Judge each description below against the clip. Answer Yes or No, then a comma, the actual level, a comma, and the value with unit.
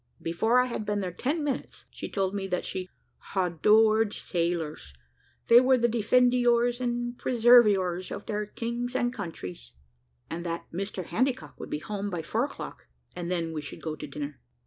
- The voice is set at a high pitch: Yes, high, 205 Hz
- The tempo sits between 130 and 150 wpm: No, average, 170 wpm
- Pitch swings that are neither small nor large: No, wide, 5.7 semitones